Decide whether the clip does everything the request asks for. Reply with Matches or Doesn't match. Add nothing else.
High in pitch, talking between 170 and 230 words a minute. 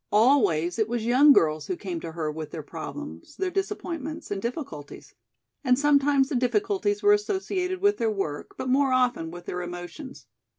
Matches